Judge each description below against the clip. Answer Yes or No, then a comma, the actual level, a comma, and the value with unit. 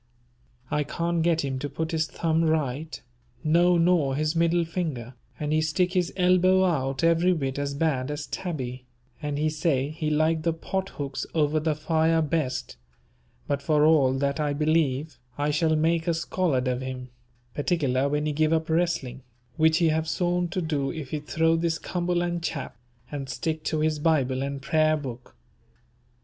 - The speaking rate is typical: Yes, average, 175 wpm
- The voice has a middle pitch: Yes, medium, 155 Hz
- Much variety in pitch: No, average, 2.8 semitones